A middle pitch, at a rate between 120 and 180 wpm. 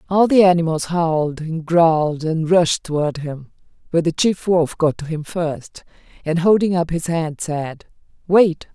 Yes: medium, 165 Hz; average, 170 wpm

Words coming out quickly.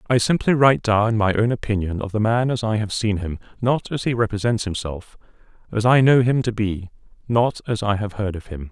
Yes: fast, 225 wpm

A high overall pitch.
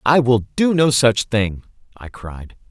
No: low, 120 Hz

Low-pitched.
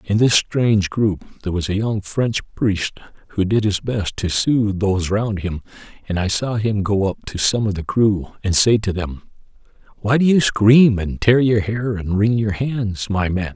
Yes: low, 105 Hz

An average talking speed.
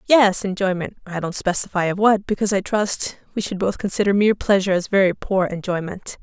Yes: average, 185 wpm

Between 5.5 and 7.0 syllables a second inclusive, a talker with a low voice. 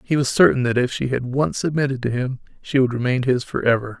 Yes: 6.0 syllables/s; low, 130 Hz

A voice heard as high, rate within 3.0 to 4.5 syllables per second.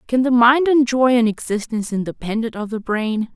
No: high, 235 Hz; 5.3 syllables/s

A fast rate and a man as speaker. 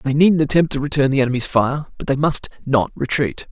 Yes: fast, 220 wpm; male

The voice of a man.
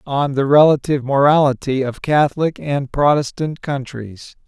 Yes: male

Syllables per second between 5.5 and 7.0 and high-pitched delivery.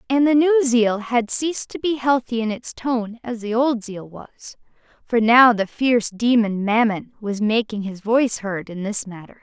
No: 4.7 syllables/s; high, 230 Hz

